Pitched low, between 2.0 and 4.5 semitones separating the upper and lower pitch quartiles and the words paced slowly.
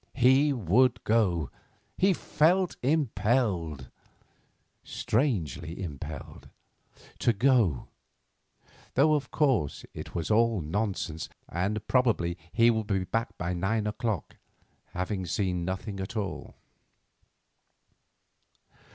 No: low, 105 Hz; wide, 5.6 semitones; slow, 90 wpm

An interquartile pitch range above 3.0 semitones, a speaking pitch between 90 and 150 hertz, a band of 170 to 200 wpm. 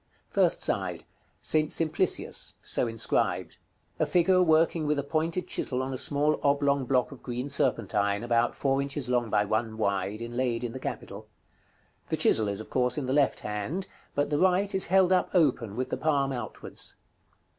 Yes: average, 4.9 semitones; low, 135 Hz; average, 185 wpm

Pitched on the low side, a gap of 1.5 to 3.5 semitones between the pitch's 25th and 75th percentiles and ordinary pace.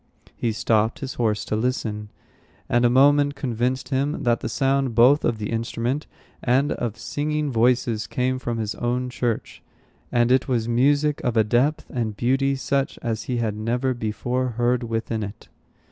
Yes: low, 120 Hz; average, 2.7 semitones; average, 170 wpm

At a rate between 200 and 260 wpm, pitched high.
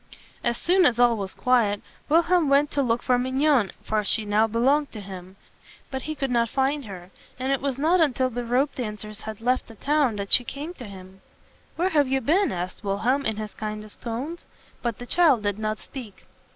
Yes: fast, 205 wpm; high, 245 Hz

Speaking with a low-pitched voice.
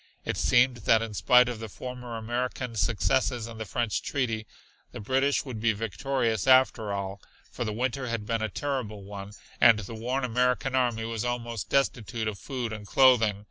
Yes: low, 115 Hz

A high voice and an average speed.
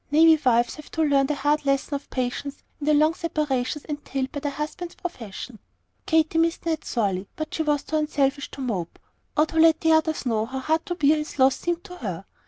No: very high, 295 Hz; fast, 215 wpm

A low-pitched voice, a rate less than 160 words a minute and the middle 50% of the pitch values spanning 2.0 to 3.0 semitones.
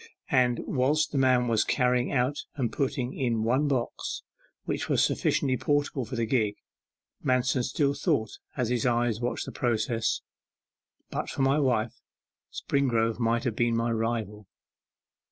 Yes: low, 125 Hz; average, 150 wpm; narrow, 2.5 semitones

